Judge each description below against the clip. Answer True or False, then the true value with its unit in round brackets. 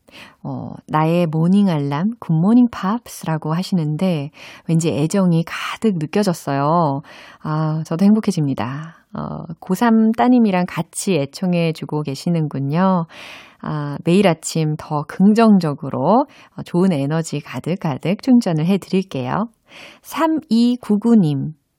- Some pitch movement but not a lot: True (4.8 semitones)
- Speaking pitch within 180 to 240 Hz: False (170 Hz)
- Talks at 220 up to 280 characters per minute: True (235 characters per minute)